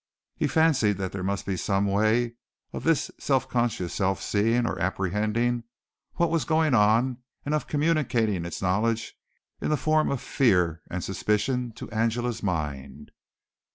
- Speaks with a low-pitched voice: Yes, low, 115 Hz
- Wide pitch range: No, average, 5.0 semitones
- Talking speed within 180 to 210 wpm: No, average, 150 wpm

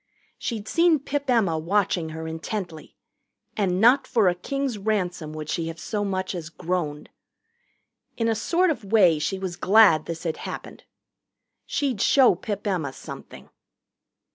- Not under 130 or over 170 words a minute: Yes, average, 150 wpm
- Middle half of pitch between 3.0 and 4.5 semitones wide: No, wide, 5.4 semitones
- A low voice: No, high, 190 Hz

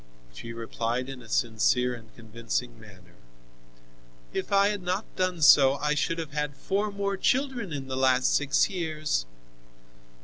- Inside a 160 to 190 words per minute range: No, average, 150 wpm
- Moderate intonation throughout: No, wide, 7.6 semitones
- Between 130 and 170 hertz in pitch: Yes, medium, 140 Hz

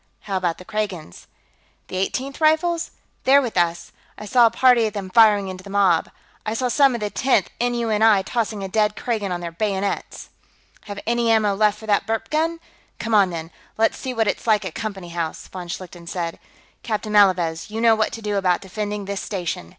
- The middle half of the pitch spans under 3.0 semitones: No, average, 3.4 semitones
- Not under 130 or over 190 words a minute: No, fast, 205 wpm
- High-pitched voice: Yes, high, 210 Hz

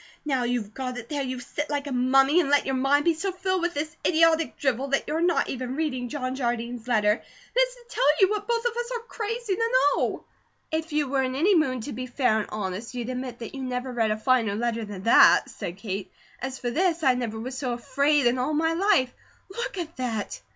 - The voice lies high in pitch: Yes, very high, 265 Hz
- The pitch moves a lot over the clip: No, average, 5.0 semitones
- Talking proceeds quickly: Yes, fast, 235 wpm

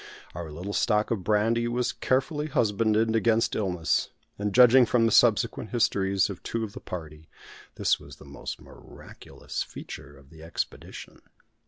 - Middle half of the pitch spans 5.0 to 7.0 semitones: No, average, 4.4 semitones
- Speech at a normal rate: Yes, average, 155 wpm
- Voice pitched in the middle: No, low, 110 Hz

